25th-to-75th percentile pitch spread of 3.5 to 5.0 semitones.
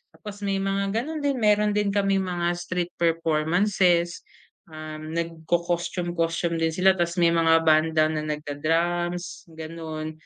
No: average, 2.9 semitones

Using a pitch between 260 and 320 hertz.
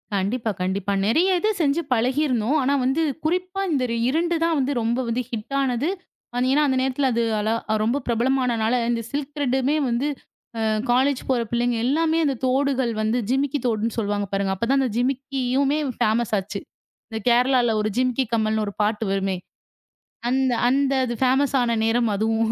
No: very high, 250 Hz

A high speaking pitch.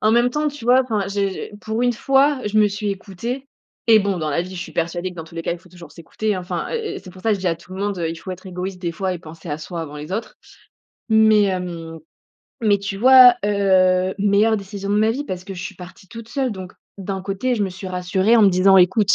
Yes: high, 195 Hz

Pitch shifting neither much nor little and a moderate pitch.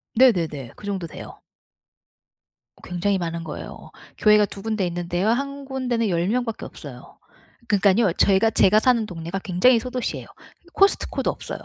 No: average, 5.0 semitones; high, 205 Hz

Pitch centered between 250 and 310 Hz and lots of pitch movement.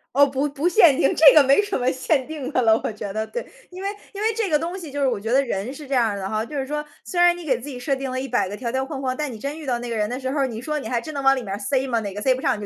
No: very high, 265 Hz; average, 4.0 semitones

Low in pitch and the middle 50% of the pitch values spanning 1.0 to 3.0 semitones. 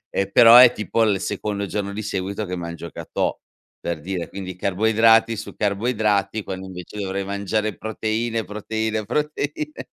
Yes: low, 105 Hz; narrow, 2.5 semitones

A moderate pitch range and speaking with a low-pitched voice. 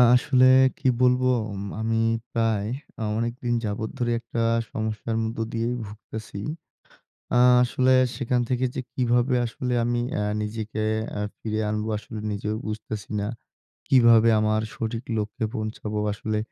No: narrow, 2.1 semitones; low, 115 Hz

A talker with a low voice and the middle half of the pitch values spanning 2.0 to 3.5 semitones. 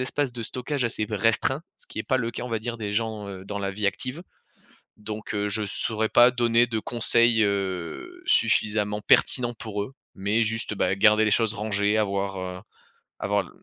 Yes: low, 110 Hz; narrow, 2.5 semitones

